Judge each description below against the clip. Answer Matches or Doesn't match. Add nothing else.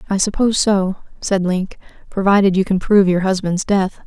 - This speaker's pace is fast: Doesn't match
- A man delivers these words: Doesn't match